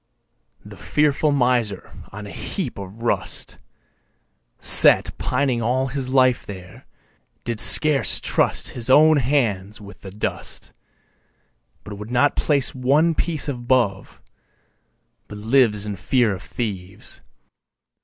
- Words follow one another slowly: Yes, slow, 125 wpm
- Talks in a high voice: No, low, 120 Hz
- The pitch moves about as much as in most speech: Yes, average, 4.8 semitones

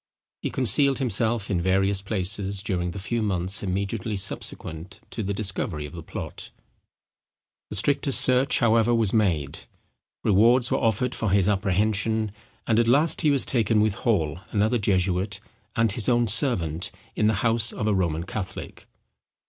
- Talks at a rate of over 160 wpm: No, average, 155 wpm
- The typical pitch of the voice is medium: No, low, 105 Hz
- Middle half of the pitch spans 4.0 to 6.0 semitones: No, average, 3.4 semitones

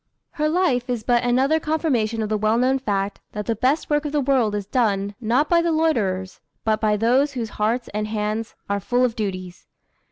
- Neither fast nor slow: No, fast, 210 wpm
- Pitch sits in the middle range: No, high, 230 Hz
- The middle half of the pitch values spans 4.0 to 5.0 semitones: Yes, average, 4.4 semitones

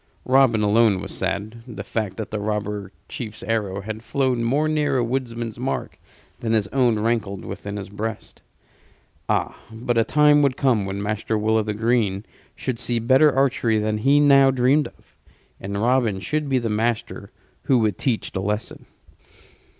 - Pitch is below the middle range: Yes, low, 115 Hz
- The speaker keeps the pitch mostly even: No, average, 3.6 semitones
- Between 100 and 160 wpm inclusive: No, average, 175 wpm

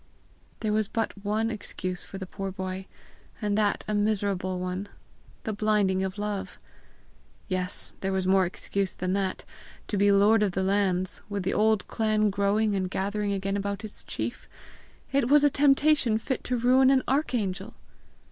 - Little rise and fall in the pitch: Yes, narrow, 2.3 semitones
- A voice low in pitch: No, high, 205 Hz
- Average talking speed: Yes, average, 170 wpm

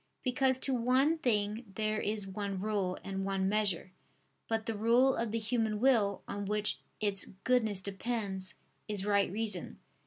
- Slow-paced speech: No, average, 155 wpm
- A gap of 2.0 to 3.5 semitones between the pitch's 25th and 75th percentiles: Yes, average, 2.8 semitones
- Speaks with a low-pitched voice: No, high, 210 Hz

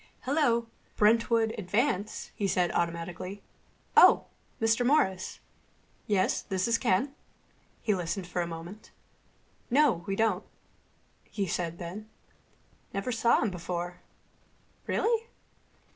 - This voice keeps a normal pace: No, slow, 110 wpm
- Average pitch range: Yes, average, 4.5 semitones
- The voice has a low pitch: No, high, 200 Hz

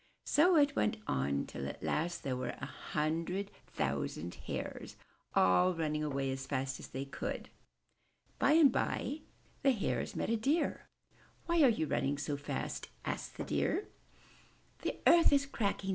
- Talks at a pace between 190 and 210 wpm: No, average, 160 wpm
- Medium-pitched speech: Yes, medium, 165 Hz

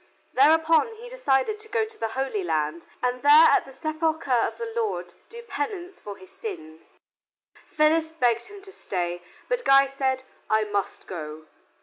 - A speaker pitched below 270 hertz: No, very high, 280 Hz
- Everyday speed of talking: Yes, average, 165 wpm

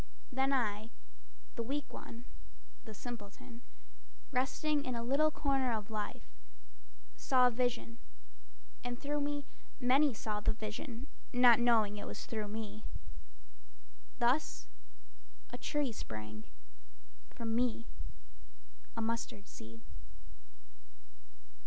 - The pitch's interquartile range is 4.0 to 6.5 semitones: No, average, 3.5 semitones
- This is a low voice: No, high, 235 Hz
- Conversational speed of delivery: No, slow, 110 wpm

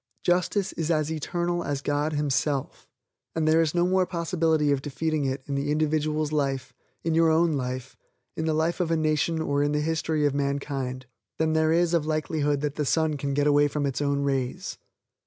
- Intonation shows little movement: Yes, narrow, 2.2 semitones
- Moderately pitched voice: Yes, medium, 150 Hz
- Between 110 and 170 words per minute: No, average, 195 wpm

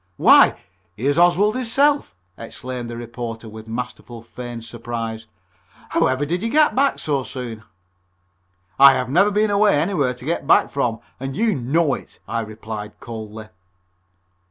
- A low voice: Yes, low, 125 Hz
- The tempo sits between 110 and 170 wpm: Yes, average, 145 wpm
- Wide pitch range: Yes, wide, 7.0 semitones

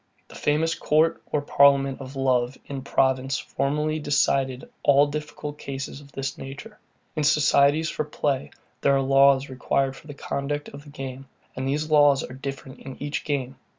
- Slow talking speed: No, average, 170 wpm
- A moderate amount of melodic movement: No, narrow, 1.7 semitones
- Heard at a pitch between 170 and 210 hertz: No, medium, 140 Hz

